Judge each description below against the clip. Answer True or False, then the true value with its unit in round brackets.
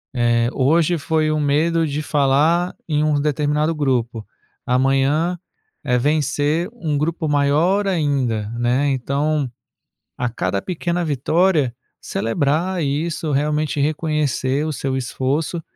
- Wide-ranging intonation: False (3.1 semitones)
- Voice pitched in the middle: True (150 Hz)